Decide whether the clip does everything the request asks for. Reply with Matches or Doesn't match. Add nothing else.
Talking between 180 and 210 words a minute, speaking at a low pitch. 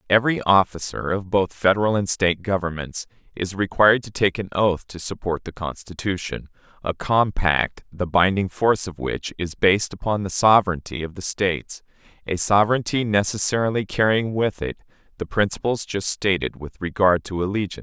Doesn't match